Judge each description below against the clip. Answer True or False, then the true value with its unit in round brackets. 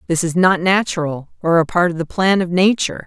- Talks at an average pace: False (235 wpm)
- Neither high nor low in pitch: True (175 Hz)